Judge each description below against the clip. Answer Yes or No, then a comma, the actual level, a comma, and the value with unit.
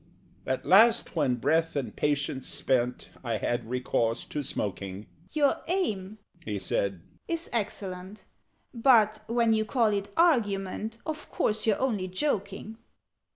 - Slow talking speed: Yes, slow, 130 wpm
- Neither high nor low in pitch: No, high, 195 Hz